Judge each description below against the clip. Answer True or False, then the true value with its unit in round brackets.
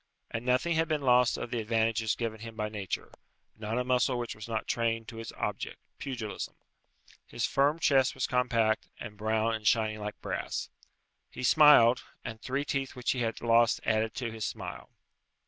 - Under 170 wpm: False (180 wpm)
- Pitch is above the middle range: False (115 Hz)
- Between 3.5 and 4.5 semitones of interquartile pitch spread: False (2.4 semitones)